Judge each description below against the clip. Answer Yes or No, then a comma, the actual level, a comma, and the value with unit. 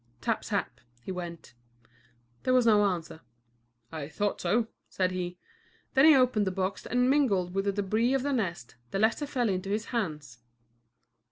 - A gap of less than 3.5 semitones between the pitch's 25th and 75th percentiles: No, average, 5.2 semitones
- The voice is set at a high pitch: Yes, high, 200 Hz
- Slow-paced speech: No, average, 170 wpm